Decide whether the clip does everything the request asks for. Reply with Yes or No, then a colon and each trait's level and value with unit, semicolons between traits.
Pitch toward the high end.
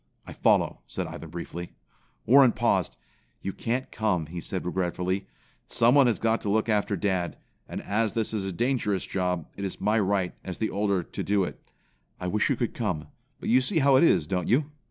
No: low, 100 Hz